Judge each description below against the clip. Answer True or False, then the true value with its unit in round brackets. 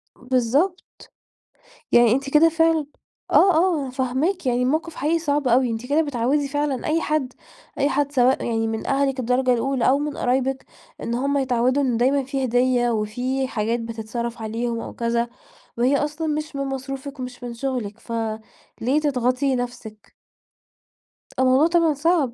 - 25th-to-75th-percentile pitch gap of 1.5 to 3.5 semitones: True (3.2 semitones)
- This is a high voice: True (260 Hz)